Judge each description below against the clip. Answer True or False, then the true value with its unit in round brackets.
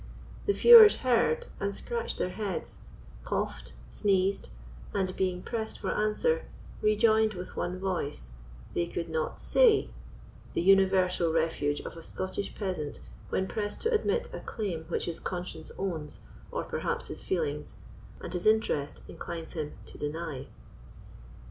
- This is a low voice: False (185 Hz)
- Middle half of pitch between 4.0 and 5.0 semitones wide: True (4.7 semitones)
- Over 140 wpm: False (135 wpm)